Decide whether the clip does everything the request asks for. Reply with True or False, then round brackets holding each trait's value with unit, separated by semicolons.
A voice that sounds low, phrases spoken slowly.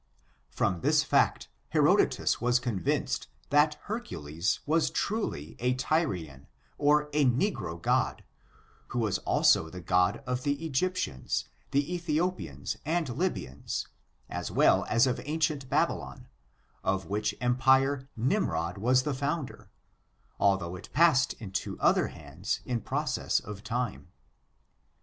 True (125 Hz; 120 wpm)